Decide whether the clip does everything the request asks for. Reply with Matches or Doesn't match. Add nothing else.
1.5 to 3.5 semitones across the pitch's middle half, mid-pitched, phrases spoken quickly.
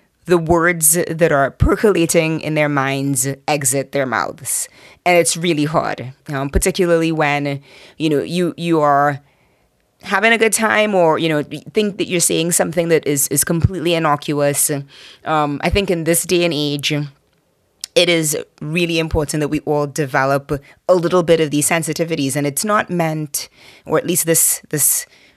Doesn't match